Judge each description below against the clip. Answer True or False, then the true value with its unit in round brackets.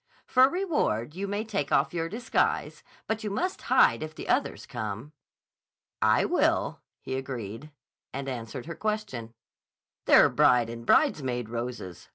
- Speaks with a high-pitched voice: False (140 Hz)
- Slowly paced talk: False (145 wpm)